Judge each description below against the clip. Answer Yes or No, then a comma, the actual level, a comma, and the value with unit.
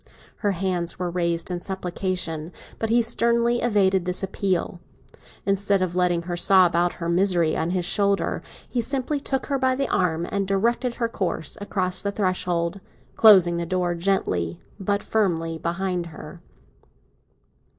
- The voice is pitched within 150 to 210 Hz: Yes, medium, 185 Hz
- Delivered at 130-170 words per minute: Yes, average, 150 wpm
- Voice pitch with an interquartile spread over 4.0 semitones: No, average, 2.9 semitones